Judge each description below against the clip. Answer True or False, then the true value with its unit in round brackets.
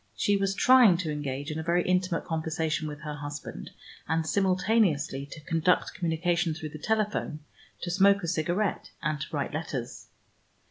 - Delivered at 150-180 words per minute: True (165 wpm)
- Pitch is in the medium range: True (165 Hz)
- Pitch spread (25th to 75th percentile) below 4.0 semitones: True (3.4 semitones)